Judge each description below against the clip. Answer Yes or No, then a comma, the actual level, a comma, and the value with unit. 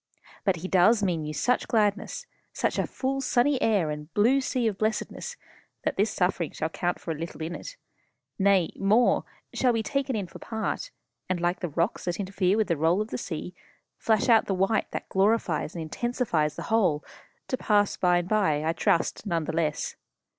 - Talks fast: No, average, 195 wpm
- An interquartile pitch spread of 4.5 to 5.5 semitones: Yes, average, 4.8 semitones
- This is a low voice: No, high, 195 Hz